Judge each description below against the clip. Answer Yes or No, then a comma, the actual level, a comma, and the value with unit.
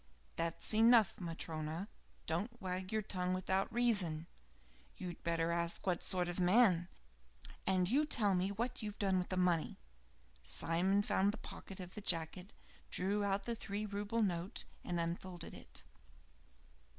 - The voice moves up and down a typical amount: Yes, average, 3.1 semitones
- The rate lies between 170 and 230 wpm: No, average, 155 wpm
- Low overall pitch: No, medium, 185 Hz